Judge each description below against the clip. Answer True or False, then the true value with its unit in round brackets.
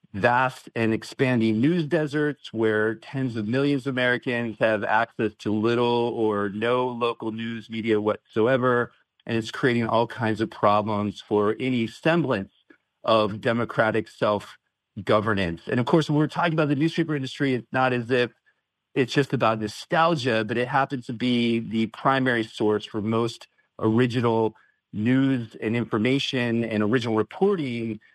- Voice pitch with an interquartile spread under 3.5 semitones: True (3.0 semitones)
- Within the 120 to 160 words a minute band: True (150 wpm)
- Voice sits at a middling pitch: False (115 Hz)